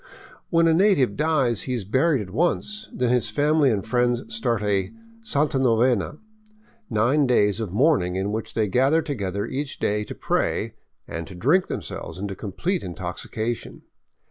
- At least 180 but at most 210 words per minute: No, average, 170 wpm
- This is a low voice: Yes, low, 120 Hz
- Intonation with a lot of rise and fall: Yes, wide, 6.6 semitones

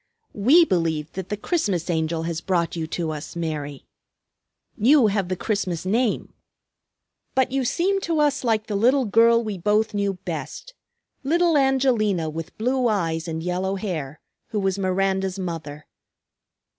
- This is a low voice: No, high, 195 Hz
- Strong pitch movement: Yes, wide, 5.9 semitones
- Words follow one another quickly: No, average, 150 wpm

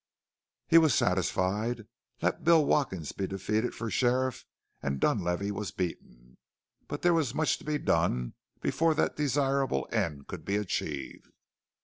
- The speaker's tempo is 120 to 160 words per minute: Yes, average, 140 wpm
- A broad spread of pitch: Yes, wide, 7.5 semitones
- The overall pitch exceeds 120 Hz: No, low, 110 Hz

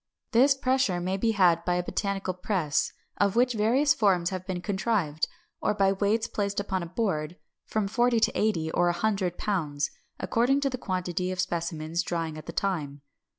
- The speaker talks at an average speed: Yes, average, 185 wpm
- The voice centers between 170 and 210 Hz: Yes, high, 190 Hz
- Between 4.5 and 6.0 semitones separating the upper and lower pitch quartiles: No, average, 3.9 semitones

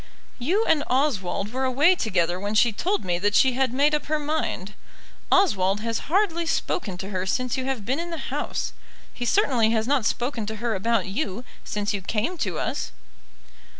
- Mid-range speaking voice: No, high, 240 Hz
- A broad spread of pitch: Yes, wide, 6.3 semitones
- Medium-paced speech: Yes, average, 190 wpm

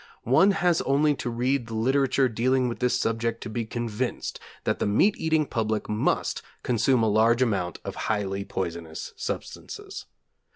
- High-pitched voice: No, low, 115 Hz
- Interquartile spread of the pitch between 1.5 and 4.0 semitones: Yes, average, 3.4 semitones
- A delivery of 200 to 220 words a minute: No, average, 160 wpm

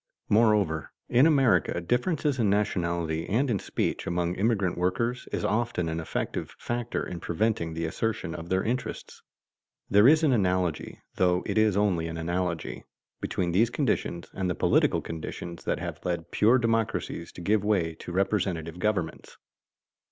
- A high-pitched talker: No, very low, 95 Hz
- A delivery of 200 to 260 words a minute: No, average, 155 wpm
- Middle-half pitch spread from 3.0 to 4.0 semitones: No, average, 4.8 semitones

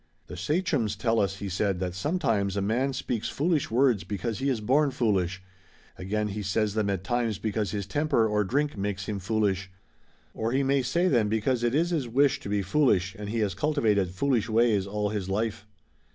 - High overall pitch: No, low, 110 Hz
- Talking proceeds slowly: No, average, 200 wpm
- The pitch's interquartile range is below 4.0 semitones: No, average, 4.5 semitones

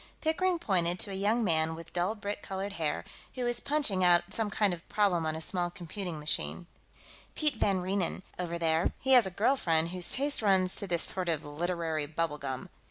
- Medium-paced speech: No, fast, 210 wpm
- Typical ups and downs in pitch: Yes, average, 3.8 semitones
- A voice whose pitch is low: No, medium, 185 Hz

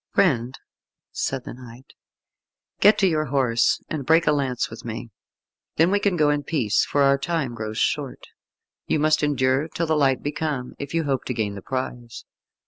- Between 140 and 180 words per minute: No, average, 190 wpm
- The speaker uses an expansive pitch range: No, average, 3.8 semitones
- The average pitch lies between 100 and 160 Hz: Yes, medium, 140 Hz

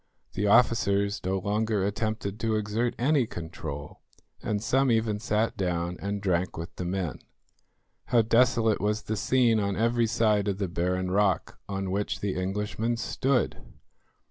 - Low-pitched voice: Yes, low, 105 Hz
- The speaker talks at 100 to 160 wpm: Yes, average, 150 wpm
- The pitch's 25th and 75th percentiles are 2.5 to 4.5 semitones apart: Yes, average, 3.0 semitones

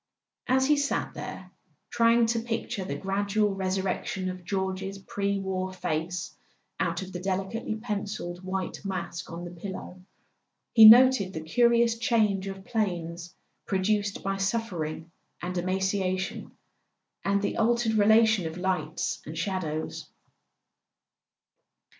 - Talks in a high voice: Yes, high, 195 Hz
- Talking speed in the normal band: No, slow, 125 wpm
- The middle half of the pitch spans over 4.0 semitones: No, average, 2.9 semitones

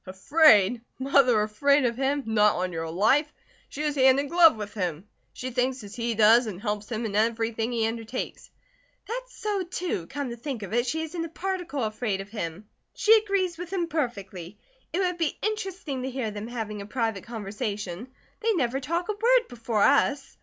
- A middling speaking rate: Yes, average, 195 wpm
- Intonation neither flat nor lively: No, wide, 6.8 semitones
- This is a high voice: Yes, high, 245 Hz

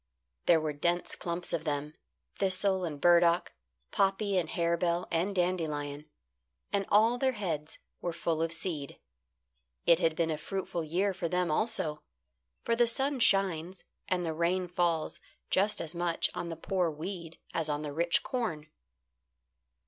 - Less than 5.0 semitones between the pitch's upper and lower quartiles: Yes, average, 2.9 semitones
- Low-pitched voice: No, medium, 170 Hz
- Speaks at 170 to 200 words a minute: No, average, 155 wpm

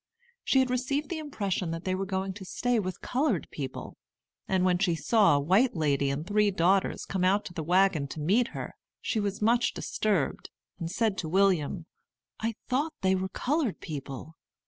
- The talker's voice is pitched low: No, high, 190 Hz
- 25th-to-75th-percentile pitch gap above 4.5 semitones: Yes, average, 5.1 semitones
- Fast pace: No, average, 190 wpm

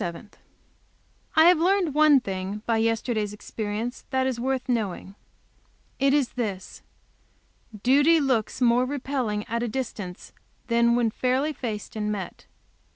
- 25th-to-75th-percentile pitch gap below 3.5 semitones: No, average, 4.0 semitones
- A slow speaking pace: Yes, slow, 130 wpm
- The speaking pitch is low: No, high, 240 Hz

